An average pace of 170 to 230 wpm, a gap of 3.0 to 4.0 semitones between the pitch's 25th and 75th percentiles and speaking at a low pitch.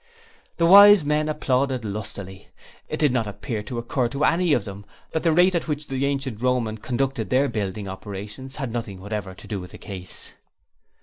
No: average, 190 wpm; wide, 5.6 semitones; low, 125 Hz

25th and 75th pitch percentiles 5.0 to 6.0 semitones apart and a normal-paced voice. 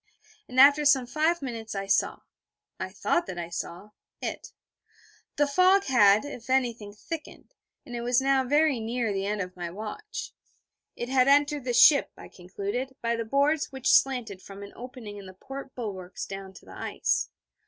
Yes: wide, 5.4 semitones; average, 180 wpm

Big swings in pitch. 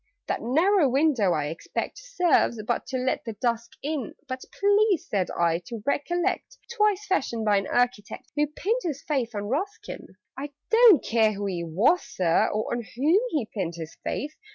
Yes: wide, 8.7 semitones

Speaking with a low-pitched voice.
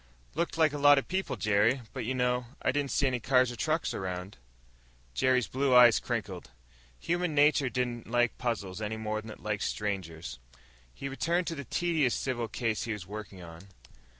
Yes: low, 120 Hz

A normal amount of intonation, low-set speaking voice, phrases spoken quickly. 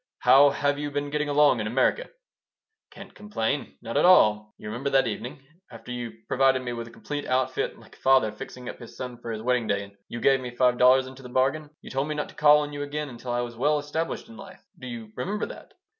Yes: average, 3.4 semitones; low, 130 Hz; fast, 245 wpm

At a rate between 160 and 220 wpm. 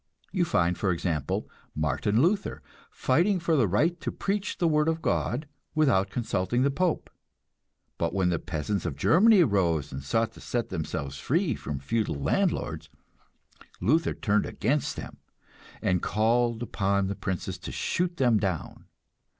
No: average, 150 wpm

